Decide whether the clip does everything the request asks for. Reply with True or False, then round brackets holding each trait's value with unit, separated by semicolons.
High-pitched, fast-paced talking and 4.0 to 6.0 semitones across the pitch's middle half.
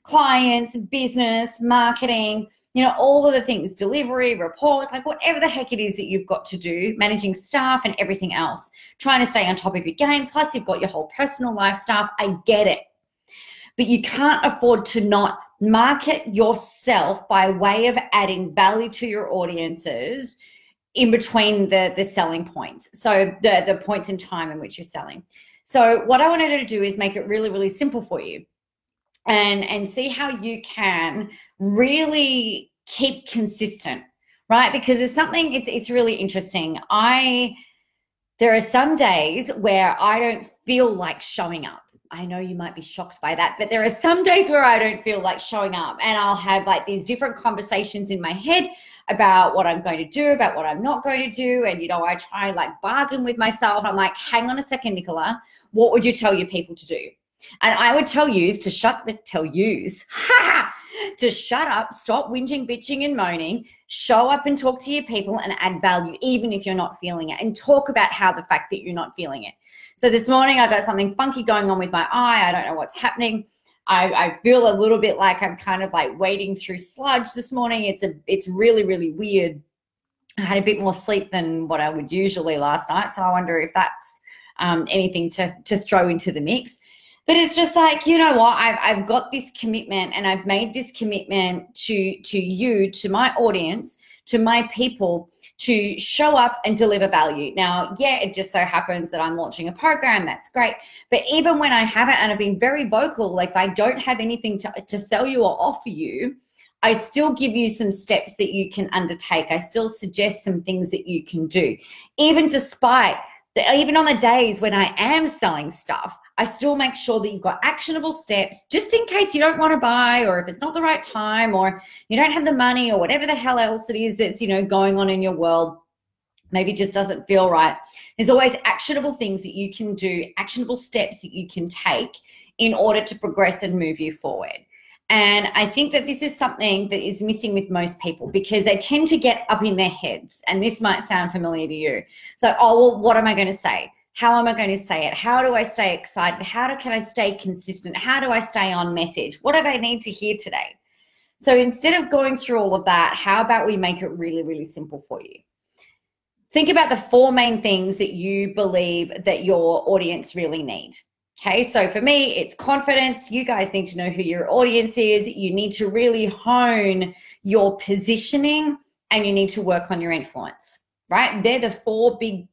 True (215 Hz; 210 wpm; 4.8 semitones)